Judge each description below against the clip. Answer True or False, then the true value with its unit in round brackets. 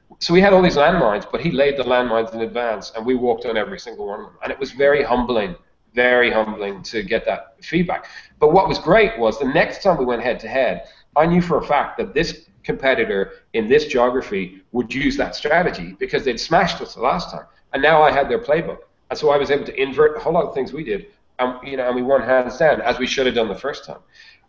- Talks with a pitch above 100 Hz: True (135 Hz)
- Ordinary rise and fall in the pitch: False (6.6 semitones)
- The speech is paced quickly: True (255 wpm)